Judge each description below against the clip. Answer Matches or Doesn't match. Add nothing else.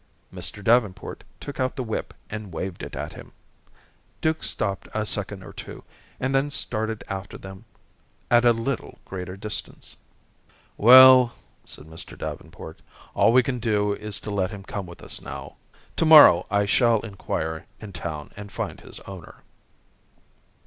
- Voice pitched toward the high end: Doesn't match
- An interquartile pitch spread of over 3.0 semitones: Matches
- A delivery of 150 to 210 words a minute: Matches